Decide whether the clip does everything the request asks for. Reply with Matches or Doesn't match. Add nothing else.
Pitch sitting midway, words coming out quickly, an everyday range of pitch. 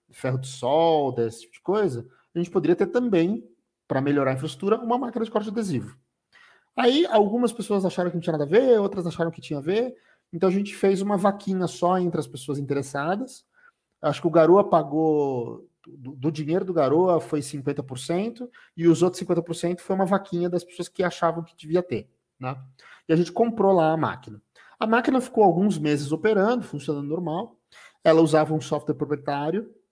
Matches